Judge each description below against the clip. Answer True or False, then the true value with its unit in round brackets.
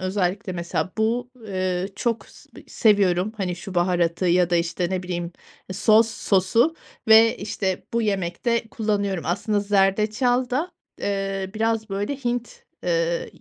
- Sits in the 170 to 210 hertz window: True (195 Hz)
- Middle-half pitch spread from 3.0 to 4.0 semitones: True (3.5 semitones)